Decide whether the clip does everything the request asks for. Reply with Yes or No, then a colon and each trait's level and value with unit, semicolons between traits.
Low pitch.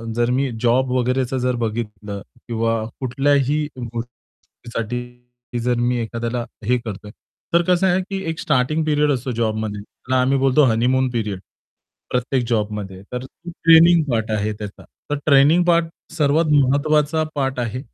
Yes: low, 125 Hz